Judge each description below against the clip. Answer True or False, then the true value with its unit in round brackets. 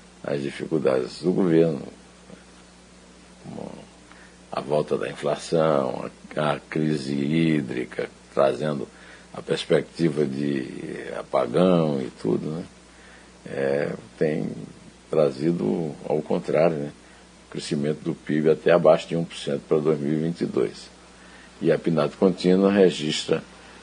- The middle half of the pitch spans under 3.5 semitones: True (3.1 semitones)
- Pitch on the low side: True (75 Hz)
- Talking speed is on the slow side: True (105 wpm)